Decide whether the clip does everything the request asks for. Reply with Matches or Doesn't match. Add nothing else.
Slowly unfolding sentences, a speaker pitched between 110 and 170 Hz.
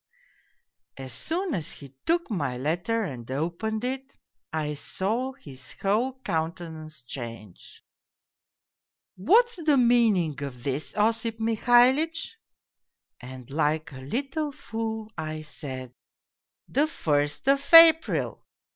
Doesn't match